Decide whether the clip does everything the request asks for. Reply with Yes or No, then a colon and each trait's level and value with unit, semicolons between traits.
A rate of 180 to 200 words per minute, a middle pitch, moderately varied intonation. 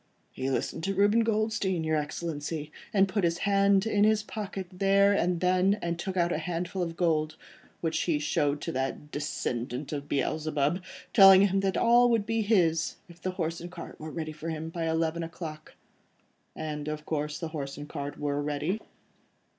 Yes: average, 185 wpm; medium, 165 Hz; average, 4.2 semitones